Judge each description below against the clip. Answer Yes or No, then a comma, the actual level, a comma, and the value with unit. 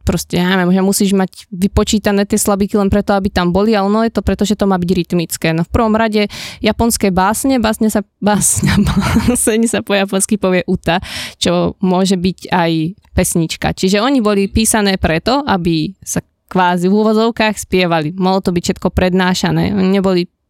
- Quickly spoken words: Yes, fast, 180 wpm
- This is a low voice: No, high, 195 Hz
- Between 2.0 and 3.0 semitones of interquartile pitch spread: Yes, average, 2.7 semitones